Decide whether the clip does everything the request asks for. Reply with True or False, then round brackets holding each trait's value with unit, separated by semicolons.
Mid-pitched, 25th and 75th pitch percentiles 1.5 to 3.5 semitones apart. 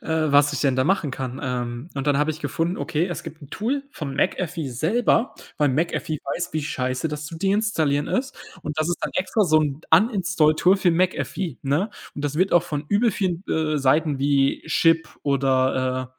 False (155 Hz; 4.4 semitones)